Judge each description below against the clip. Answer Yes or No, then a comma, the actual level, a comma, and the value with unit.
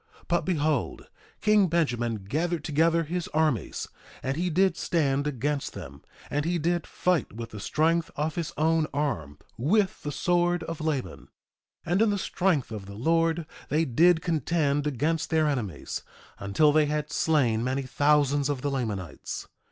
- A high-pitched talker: No, medium, 150 Hz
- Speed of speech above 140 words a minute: Yes, average, 160 wpm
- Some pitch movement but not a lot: Yes, average, 3.7 semitones